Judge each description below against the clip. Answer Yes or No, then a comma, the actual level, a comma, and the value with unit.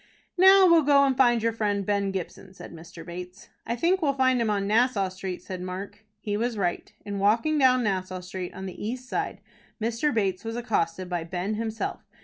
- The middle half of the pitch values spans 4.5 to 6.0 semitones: Yes, average, 4.9 semitones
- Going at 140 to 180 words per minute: No, average, 200 wpm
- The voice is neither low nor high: No, high, 210 Hz